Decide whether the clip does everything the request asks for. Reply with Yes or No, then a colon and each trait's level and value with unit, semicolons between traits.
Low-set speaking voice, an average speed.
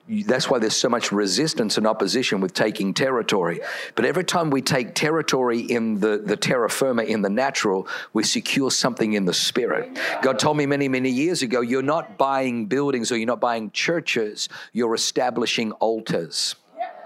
Yes: low, 130 Hz; average, 175 wpm